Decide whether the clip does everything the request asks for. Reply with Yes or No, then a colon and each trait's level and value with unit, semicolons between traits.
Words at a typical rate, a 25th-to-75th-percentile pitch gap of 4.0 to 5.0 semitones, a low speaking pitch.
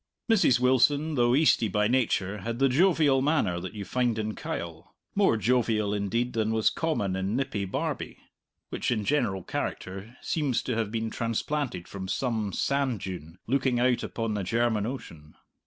Yes: average, 165 wpm; average, 4.3 semitones; low, 115 Hz